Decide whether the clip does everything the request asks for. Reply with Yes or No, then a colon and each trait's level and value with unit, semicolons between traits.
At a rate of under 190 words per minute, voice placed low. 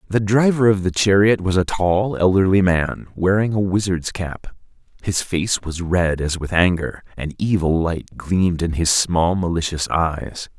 Yes: average, 170 wpm; very low, 90 Hz